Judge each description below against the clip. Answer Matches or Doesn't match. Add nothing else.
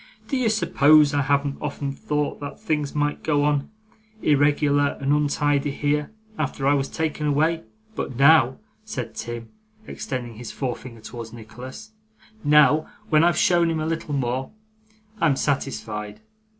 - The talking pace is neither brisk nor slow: Matches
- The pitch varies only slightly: Matches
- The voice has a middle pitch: Matches